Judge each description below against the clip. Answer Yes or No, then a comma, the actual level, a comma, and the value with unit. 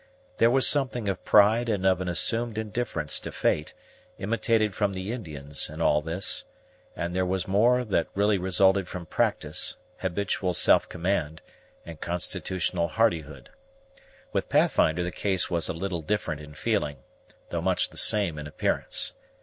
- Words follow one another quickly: No, average, 155 wpm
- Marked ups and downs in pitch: No, average, 4.1 semitones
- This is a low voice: Yes, very low, 95 Hz